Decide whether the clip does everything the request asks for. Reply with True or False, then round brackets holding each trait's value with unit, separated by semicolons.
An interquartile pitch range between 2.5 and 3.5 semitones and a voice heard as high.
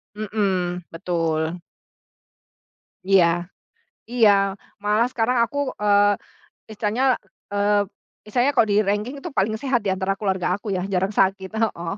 True (2.8 semitones; 205 Hz)